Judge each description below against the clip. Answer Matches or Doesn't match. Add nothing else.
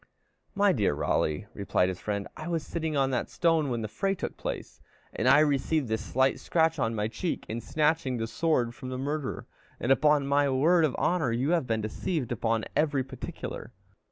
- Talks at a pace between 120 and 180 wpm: Doesn't match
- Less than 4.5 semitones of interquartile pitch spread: Doesn't match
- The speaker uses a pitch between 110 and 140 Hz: Matches